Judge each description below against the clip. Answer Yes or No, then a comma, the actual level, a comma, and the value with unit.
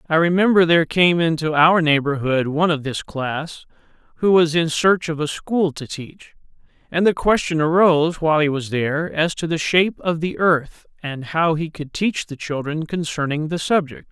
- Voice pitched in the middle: Yes, medium, 160 Hz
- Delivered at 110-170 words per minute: No, average, 190 wpm